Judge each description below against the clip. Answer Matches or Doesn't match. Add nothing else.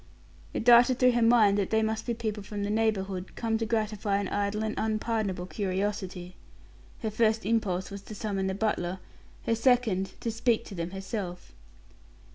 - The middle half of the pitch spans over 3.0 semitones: Doesn't match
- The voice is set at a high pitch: Matches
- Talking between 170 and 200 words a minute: Matches